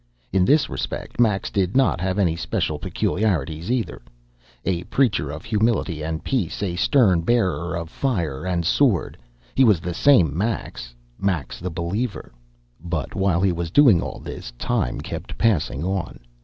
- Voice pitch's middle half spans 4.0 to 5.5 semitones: Yes, average, 4.8 semitones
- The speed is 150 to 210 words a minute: Yes, average, 155 wpm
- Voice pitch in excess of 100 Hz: No, very low, 95 Hz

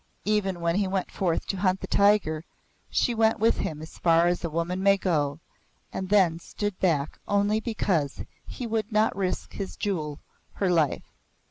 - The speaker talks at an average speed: Yes, average, 175 wpm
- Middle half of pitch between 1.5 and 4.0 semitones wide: Yes, average, 3.7 semitones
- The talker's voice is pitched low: No, high, 190 Hz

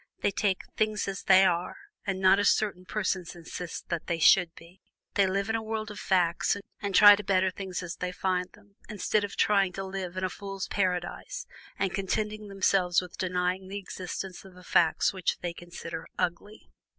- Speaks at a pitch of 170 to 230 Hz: Yes, high, 190 Hz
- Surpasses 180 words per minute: Yes, average, 195 wpm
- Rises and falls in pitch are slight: Yes, narrow, 2.0 semitones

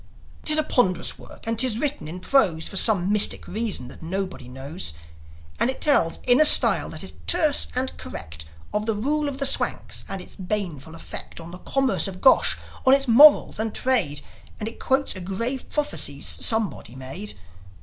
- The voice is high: Yes, high, 215 Hz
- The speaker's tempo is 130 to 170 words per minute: No, average, 185 wpm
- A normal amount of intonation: No, wide, 7.1 semitones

